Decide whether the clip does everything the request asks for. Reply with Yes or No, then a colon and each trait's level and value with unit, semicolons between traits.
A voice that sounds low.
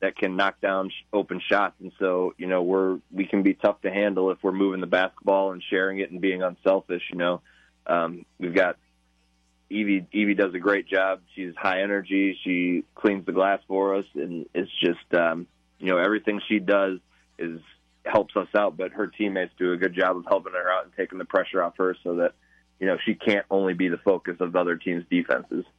Yes: very low, 95 Hz